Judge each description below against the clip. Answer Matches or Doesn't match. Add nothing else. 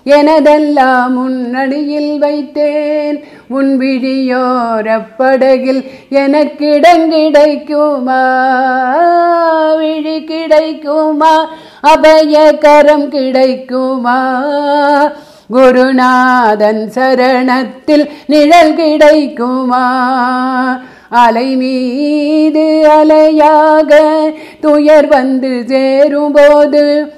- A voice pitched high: Matches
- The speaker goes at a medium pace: Doesn't match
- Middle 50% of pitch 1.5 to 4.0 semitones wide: Matches